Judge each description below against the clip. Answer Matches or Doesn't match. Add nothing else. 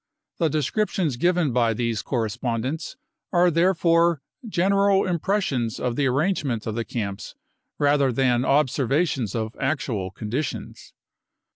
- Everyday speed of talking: Doesn't match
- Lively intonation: Matches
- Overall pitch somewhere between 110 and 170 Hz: Matches